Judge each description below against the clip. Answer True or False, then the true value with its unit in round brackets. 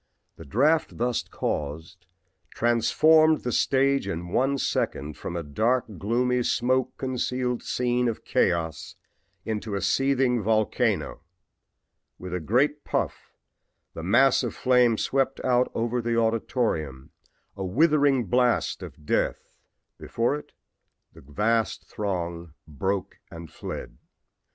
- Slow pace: True (120 wpm)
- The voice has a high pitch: False (115 Hz)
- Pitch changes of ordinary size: False (6.0 semitones)